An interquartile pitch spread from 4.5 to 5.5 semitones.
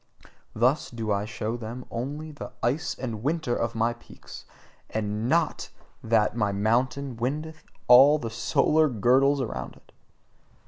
No: average, 4.0 semitones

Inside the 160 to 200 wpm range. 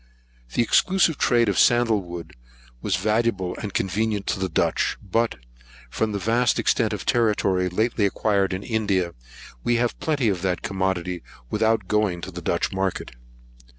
No: average, 150 wpm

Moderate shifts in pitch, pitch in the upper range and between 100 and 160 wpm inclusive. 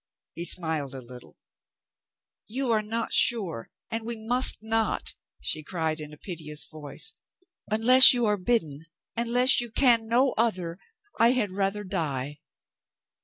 No: wide, 6.8 semitones; high, 210 Hz; average, 140 wpm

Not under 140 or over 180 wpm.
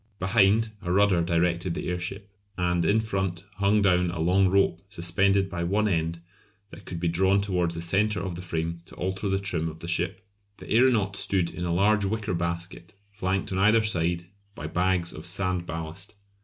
No: average, 190 wpm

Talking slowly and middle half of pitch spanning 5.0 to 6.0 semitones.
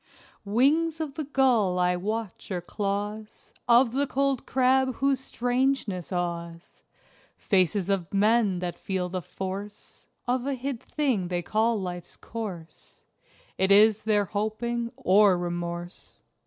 Yes: slow, 130 wpm; wide, 5.6 semitones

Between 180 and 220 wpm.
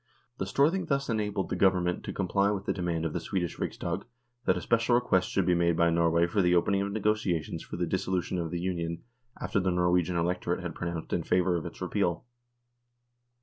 Yes: fast, 205 wpm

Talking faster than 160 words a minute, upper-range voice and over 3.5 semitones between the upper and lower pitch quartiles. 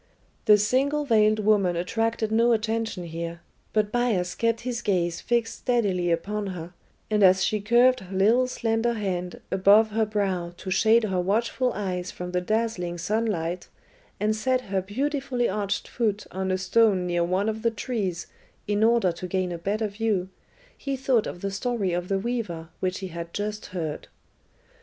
Yes: average, 170 wpm; high, 205 Hz; average, 3.9 semitones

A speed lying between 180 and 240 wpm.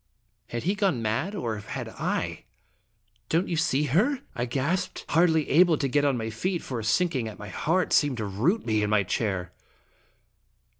Yes: average, 190 wpm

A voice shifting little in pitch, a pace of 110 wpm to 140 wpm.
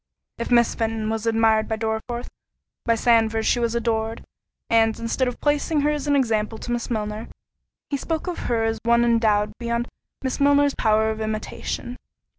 No: narrow, 1.8 semitones; average, 175 wpm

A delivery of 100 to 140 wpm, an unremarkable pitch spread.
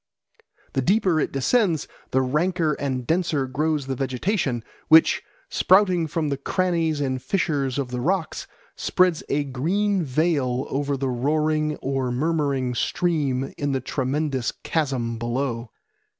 Yes: slow, 135 wpm; average, 3.8 semitones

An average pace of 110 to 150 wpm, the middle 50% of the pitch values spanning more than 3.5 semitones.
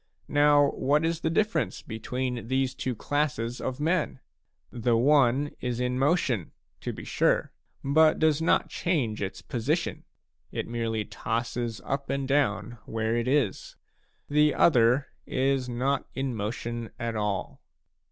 Yes: average, 140 wpm; average, 3.9 semitones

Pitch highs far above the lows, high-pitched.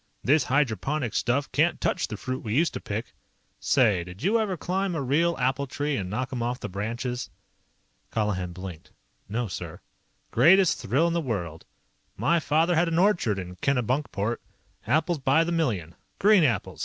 No: wide, 7.2 semitones; low, 130 Hz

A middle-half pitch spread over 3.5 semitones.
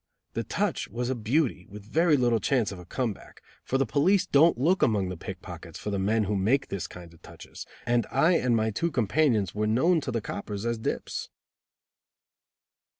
Yes: average, 5.1 semitones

